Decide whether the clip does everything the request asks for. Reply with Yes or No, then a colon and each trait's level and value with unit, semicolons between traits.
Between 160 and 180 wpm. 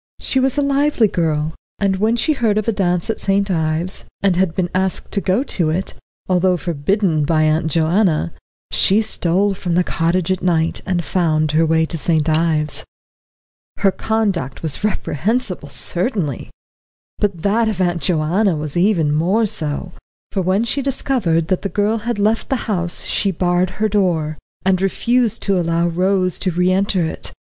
Yes: average, 175 wpm